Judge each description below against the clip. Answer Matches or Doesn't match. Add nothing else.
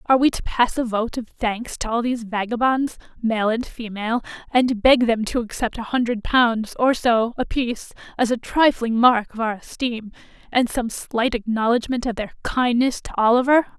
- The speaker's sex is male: Doesn't match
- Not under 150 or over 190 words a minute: Matches